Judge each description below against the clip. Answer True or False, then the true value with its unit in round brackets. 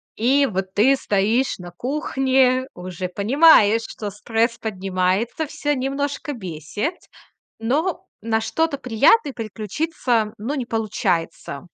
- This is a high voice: True (230 Hz)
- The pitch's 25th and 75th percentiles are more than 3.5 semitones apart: True (5.4 semitones)